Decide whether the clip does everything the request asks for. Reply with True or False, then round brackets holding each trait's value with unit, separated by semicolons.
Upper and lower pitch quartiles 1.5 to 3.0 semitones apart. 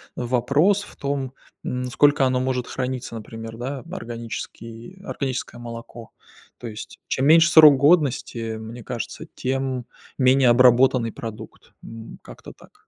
True (2.7 semitones)